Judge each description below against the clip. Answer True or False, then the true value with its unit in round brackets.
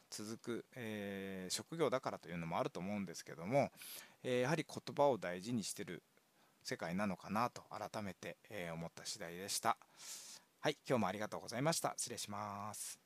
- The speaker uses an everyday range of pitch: True (5.0 semitones)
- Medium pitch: False (105 Hz)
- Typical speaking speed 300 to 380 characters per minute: True (370 characters per minute)